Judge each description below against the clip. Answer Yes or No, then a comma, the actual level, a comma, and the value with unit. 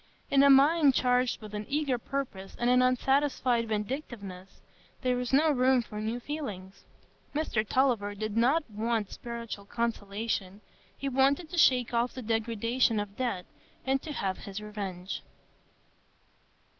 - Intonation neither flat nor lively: Yes, average, 4.1 semitones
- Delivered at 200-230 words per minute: No, average, 140 wpm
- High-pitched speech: Yes, high, 235 Hz